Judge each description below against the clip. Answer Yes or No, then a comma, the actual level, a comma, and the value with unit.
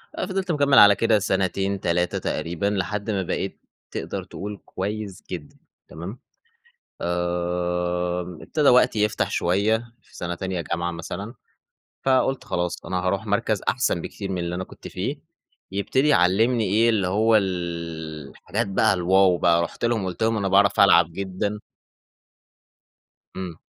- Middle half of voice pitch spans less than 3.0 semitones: No, average, 3.3 semitones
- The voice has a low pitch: Yes, very low, 95 Hz